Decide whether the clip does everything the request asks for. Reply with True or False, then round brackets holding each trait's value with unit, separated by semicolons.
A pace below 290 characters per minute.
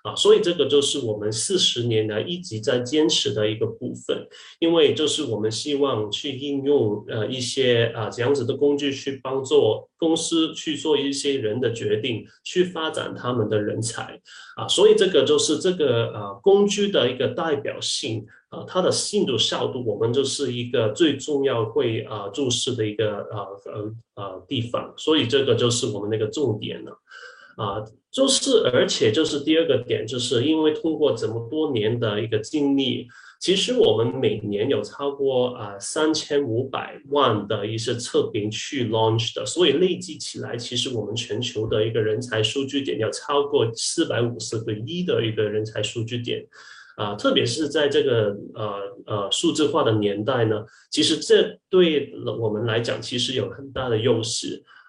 True (275 characters per minute)